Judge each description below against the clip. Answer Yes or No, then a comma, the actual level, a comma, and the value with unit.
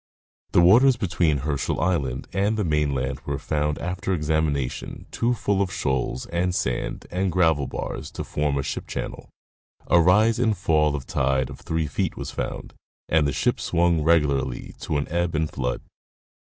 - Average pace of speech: Yes, average, 170 wpm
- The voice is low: Yes, very low, 80 Hz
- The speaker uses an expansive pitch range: No, average, 4.3 semitones